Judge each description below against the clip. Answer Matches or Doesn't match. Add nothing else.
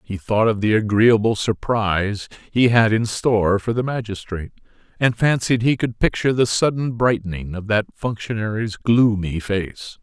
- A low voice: Matches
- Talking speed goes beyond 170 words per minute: Doesn't match